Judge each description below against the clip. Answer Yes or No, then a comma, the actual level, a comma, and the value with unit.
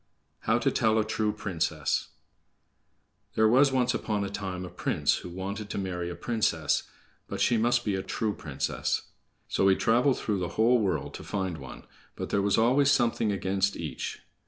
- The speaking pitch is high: No, low, 100 Hz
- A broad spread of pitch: No, average, 3.3 semitones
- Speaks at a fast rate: No, average, 180 wpm